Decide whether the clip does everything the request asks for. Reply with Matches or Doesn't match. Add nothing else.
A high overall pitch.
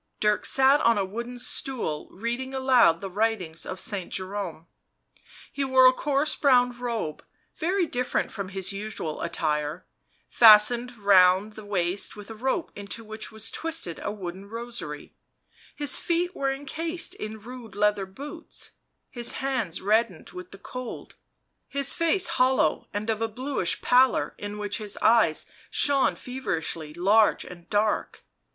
Matches